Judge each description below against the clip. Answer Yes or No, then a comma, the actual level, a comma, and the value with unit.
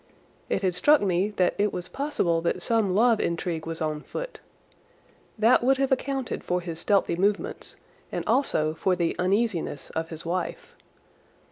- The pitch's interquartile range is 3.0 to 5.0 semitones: No, wide, 5.4 semitones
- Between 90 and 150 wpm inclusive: No, average, 160 wpm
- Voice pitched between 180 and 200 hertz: Yes, medium, 185 Hz